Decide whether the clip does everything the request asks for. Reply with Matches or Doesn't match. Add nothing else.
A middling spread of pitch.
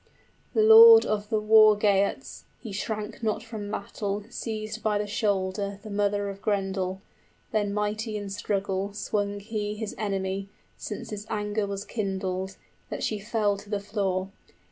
Doesn't match